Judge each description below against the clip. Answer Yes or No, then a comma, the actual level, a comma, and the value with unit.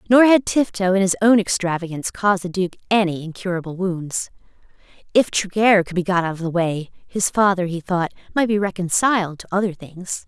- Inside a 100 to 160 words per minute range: No, average, 185 wpm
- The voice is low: No, high, 190 Hz